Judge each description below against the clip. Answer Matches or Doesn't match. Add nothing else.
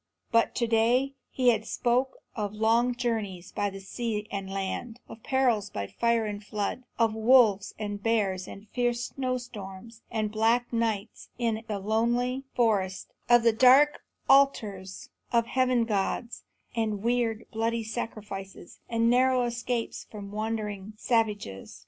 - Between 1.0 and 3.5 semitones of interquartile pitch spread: Matches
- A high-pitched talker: Matches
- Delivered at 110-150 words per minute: Matches